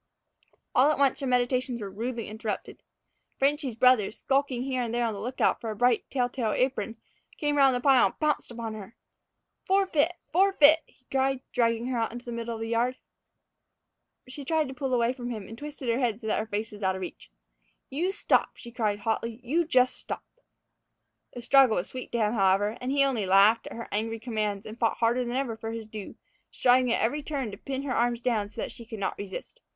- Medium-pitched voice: No, high, 240 Hz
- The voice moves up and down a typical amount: Yes, average, 3.2 semitones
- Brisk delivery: Yes, fast, 220 wpm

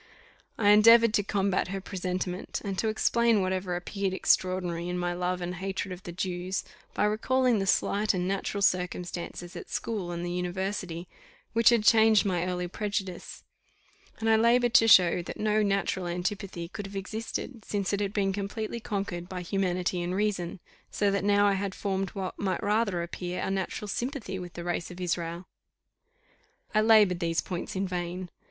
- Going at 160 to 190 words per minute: Yes, average, 175 wpm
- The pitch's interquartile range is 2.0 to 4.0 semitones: Yes, narrow, 2.6 semitones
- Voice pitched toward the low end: No, high, 190 Hz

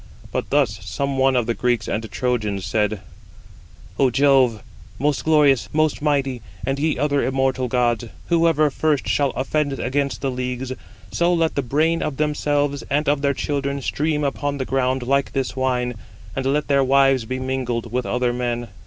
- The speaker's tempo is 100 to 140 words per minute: No, average, 170 wpm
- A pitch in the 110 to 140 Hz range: Yes, low, 135 Hz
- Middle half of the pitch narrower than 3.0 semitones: Yes, narrow, 2.6 semitones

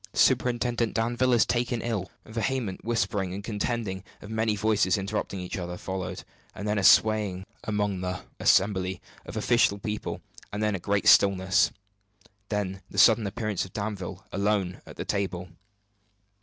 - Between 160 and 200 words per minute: No, average, 145 wpm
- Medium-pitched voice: No, low, 100 Hz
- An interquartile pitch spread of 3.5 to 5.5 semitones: No, average, 2.7 semitones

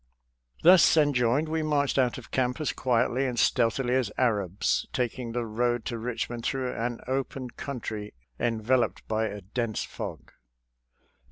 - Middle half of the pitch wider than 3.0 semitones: No, narrow, 2.4 semitones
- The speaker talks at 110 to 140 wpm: No, average, 150 wpm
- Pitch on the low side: Yes, low, 125 Hz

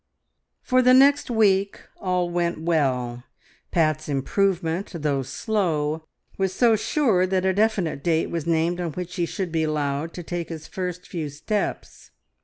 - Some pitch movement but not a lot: Yes, average, 3.6 semitones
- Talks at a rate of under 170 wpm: Yes, average, 155 wpm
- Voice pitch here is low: No, medium, 175 Hz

